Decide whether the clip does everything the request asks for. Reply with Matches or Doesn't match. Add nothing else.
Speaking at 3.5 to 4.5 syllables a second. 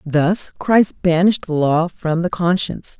Matches